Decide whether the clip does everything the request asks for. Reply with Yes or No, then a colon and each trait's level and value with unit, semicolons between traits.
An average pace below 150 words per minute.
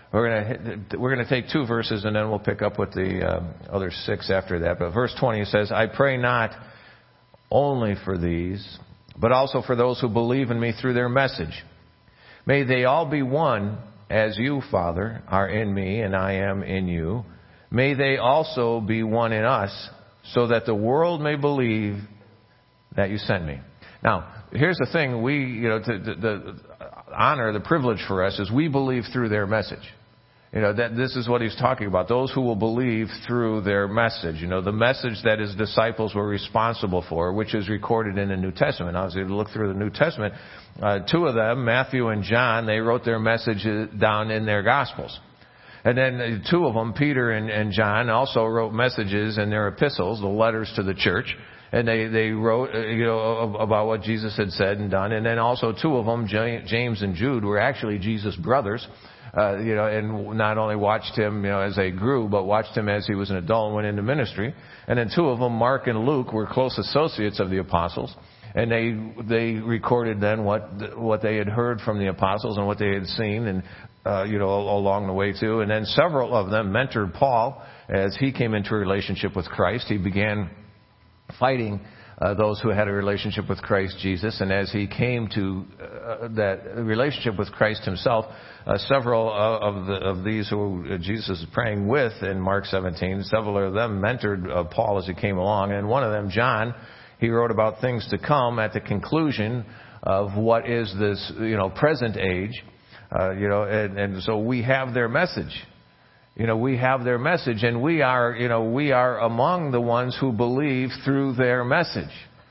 No: fast, 205 wpm